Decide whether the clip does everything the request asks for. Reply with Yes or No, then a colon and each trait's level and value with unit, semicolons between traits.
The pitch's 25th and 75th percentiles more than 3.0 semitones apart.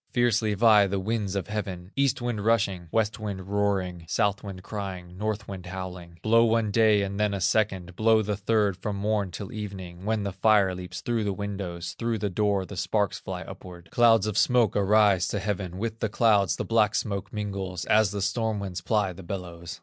No: narrow, 2.6 semitones